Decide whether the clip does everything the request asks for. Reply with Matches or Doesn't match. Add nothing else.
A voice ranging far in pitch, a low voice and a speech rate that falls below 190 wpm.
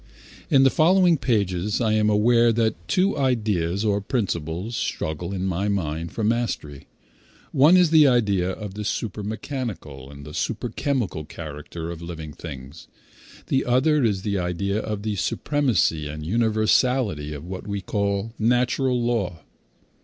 Matches